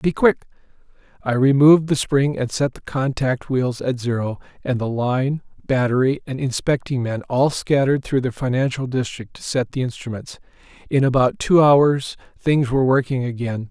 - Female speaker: No, male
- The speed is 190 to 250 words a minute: No, average, 165 wpm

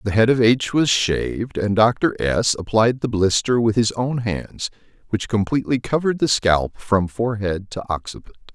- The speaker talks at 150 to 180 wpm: Yes, average, 175 wpm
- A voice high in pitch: No, low, 110 Hz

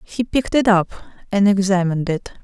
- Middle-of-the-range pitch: No, high, 200 Hz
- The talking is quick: No, average, 175 wpm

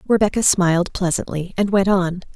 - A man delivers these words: No, female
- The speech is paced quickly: No, average, 155 wpm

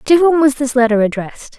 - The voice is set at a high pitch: Yes, very high, 265 Hz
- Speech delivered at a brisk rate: Yes, fast, 230 wpm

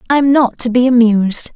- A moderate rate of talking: Yes, average, 195 wpm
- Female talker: Yes, female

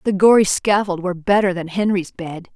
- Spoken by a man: No, female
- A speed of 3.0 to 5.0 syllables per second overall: No, 5.5 syllables/s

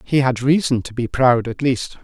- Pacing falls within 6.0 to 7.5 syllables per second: No, 4.7 syllables/s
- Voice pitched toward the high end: No, low, 125 Hz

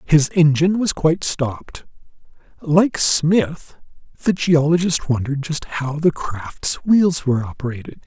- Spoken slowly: Yes, slow, 125 wpm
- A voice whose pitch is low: No, medium, 155 Hz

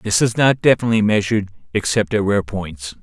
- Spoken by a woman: No, male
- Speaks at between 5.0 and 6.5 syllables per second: Yes, 5.9 syllables/s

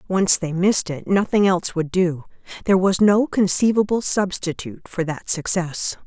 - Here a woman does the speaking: Yes, female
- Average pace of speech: Yes, average, 160 wpm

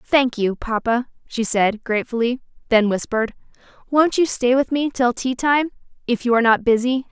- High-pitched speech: Yes, high, 245 Hz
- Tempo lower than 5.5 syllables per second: Yes, 5.2 syllables/s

